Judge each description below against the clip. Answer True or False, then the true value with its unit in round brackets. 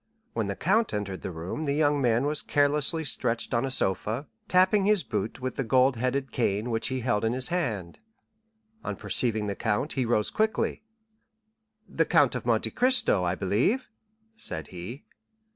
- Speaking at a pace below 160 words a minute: False (175 wpm)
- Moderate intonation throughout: False (5.9 semitones)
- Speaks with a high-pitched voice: False (125 Hz)